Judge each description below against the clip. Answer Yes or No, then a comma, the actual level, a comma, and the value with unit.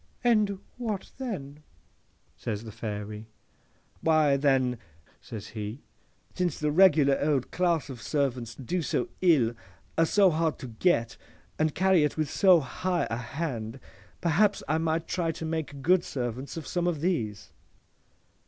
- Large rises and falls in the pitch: Yes, wide, 6.1 semitones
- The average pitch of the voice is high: No, medium, 150 Hz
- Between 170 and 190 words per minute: No, average, 145 wpm